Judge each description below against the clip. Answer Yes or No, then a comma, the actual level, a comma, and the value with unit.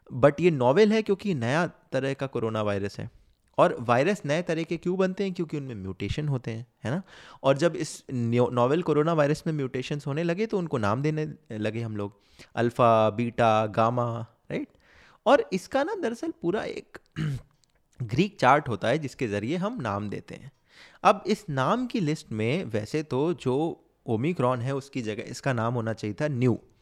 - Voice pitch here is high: No, low, 135 Hz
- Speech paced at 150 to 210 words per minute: Yes, average, 185 wpm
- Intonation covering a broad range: Yes, wide, 6.4 semitones